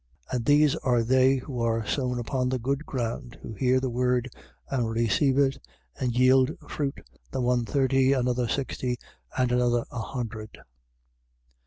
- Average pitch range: No, narrow, 1.7 semitones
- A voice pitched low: Yes, low, 125 Hz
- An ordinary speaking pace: Yes, average, 160 wpm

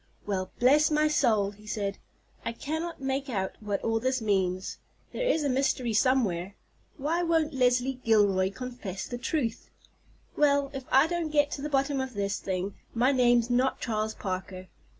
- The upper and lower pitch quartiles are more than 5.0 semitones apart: Yes, wide, 5.5 semitones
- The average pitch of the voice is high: Yes, very high, 250 Hz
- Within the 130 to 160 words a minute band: No, average, 170 wpm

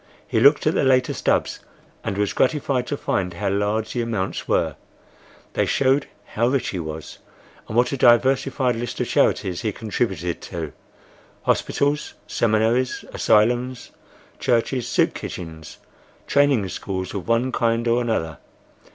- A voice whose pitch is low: Yes, low, 115 Hz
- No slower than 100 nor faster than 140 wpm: Yes, slow, 135 wpm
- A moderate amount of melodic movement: Yes, average, 4.6 semitones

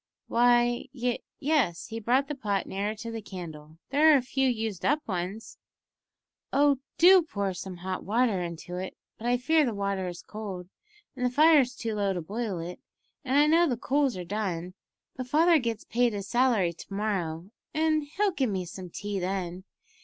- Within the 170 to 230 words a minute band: Yes, average, 190 wpm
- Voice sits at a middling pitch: No, high, 220 Hz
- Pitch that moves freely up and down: Yes, wide, 5.9 semitones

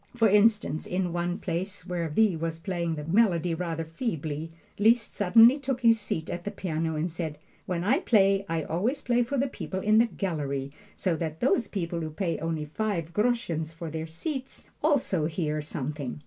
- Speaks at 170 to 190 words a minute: Yes, average, 185 wpm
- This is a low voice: No, medium, 175 Hz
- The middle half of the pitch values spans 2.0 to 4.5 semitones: No, average, 5.2 semitones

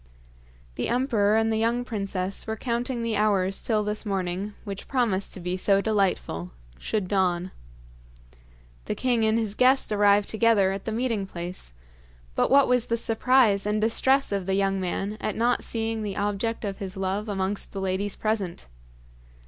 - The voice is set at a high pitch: Yes, high, 210 Hz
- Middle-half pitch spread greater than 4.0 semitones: No, average, 2.7 semitones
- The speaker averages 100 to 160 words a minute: No, average, 170 wpm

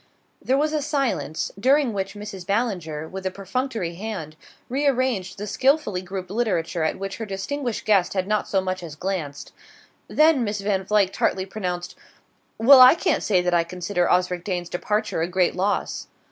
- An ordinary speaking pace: Yes, average, 175 wpm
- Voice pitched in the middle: No, high, 195 Hz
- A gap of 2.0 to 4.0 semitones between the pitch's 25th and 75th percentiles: No, average, 4.5 semitones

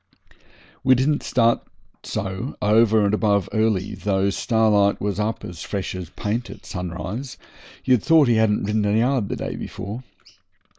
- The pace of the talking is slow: No, average, 155 wpm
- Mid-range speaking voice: No, low, 105 Hz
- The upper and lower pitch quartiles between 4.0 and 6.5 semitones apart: No, average, 2.8 semitones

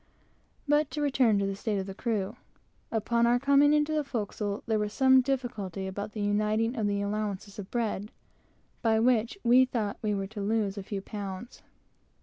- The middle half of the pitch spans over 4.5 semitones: No, average, 3.4 semitones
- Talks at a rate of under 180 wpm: No, average, 185 wpm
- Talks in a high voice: Yes, high, 215 Hz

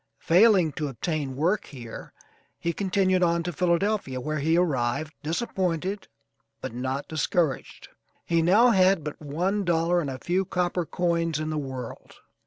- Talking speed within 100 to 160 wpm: Yes, average, 150 wpm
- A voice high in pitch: No, medium, 170 Hz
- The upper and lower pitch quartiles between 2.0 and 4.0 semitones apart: Yes, average, 3.6 semitones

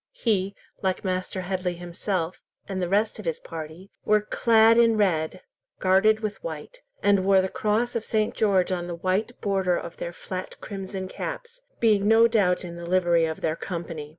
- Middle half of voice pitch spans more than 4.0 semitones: No, average, 3.3 semitones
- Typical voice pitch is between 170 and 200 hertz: Yes, high, 190 Hz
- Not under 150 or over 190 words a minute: Yes, average, 180 wpm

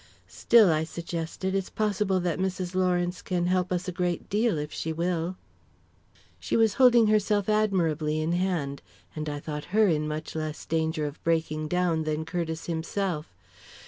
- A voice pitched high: No, medium, 175 Hz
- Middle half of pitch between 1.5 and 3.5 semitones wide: Yes, average, 3.1 semitones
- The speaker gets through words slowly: No, average, 165 wpm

